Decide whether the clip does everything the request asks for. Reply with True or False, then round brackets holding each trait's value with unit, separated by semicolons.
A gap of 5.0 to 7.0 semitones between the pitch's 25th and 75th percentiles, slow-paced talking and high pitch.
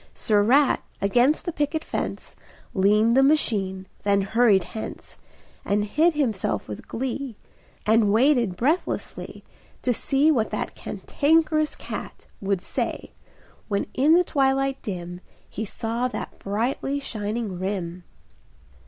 True (5.6 semitones; 125 wpm; 230 Hz)